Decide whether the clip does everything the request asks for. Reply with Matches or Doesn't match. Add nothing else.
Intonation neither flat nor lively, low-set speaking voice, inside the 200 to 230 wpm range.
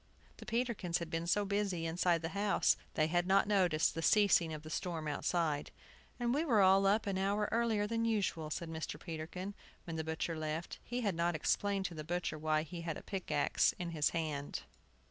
Doesn't match